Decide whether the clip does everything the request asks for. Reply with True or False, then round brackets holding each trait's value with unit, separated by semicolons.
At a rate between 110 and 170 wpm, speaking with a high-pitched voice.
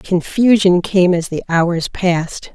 False (140 wpm; 180 Hz)